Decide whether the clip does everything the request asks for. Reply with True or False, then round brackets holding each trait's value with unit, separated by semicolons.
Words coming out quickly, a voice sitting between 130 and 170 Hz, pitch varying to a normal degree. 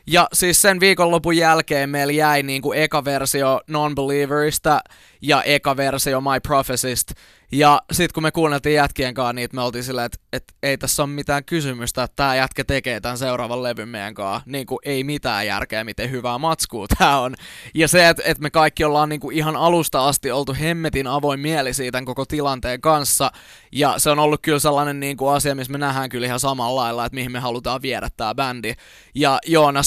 True (190 wpm; 140 Hz; 3.0 semitones)